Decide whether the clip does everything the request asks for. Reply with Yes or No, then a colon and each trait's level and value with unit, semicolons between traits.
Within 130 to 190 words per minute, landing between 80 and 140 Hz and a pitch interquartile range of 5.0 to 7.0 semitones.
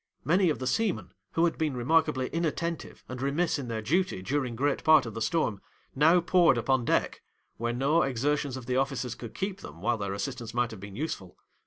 No: fast, 205 wpm; low, 135 Hz; average, 5.3 semitones